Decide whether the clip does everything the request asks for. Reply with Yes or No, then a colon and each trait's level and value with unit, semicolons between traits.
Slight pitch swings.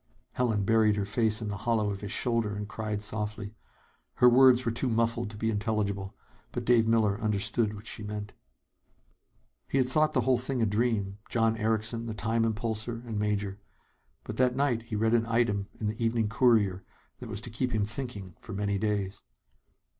Yes: narrow, 2.1 semitones